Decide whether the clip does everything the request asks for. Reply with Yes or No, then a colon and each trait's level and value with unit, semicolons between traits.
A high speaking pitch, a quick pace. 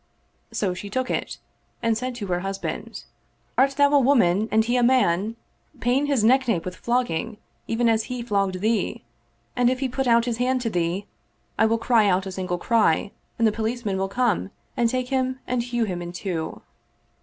Yes: high, 230 Hz; fast, 210 wpm